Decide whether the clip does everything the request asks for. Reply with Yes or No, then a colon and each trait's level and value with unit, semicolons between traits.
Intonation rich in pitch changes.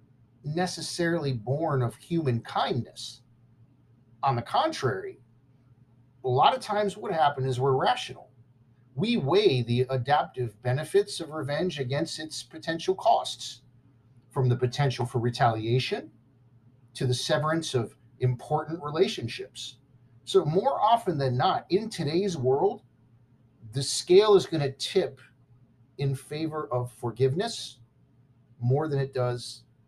No: average, 4.3 semitones